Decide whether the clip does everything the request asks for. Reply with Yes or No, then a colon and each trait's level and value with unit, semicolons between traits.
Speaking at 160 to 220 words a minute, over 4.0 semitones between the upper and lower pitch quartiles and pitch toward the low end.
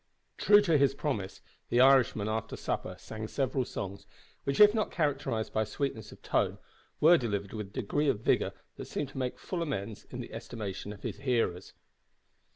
Yes: average, 180 wpm; average, 5.1 semitones; low, 125 Hz